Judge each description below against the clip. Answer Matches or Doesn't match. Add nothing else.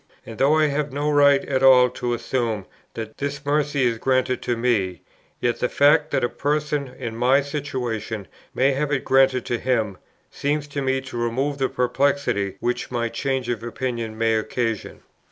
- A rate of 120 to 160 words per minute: Doesn't match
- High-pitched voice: Doesn't match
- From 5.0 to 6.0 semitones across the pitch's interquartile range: Doesn't match